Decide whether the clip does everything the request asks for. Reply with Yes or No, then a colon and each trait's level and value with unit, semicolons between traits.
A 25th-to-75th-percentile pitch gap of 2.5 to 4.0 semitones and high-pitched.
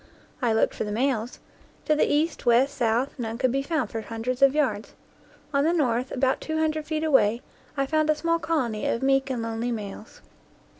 No: average, 4.7 semitones; very high, 265 Hz